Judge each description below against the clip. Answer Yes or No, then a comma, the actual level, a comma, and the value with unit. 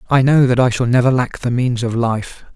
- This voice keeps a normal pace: No, fast, 260 wpm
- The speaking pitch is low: Yes, low, 120 Hz